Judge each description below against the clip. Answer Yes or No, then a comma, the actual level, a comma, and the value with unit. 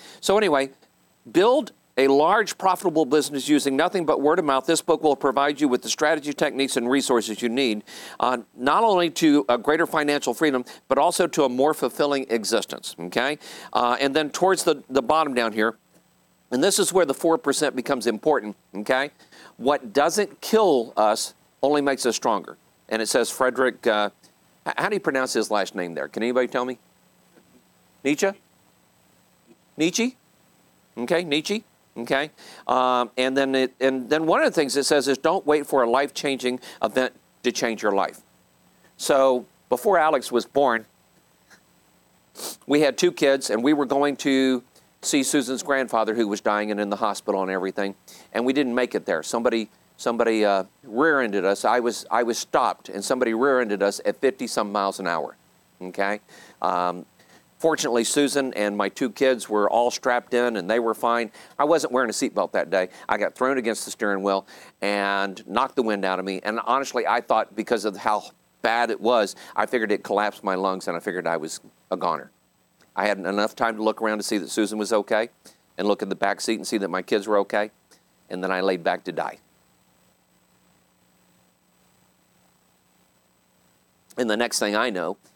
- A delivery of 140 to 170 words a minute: No, average, 185 wpm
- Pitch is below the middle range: Yes, low, 125 Hz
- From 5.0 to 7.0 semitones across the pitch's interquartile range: Yes, average, 5.3 semitones